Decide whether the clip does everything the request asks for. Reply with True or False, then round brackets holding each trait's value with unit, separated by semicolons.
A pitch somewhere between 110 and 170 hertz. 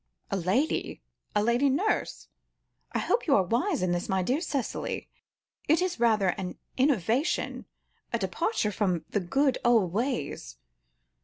False (235 Hz)